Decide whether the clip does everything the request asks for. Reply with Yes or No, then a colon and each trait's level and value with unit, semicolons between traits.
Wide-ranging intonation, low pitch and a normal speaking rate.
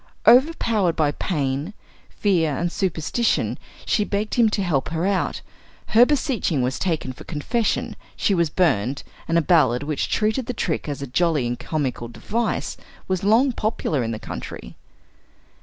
No: wide, 7.1 semitones; medium, 170 Hz; average, 155 wpm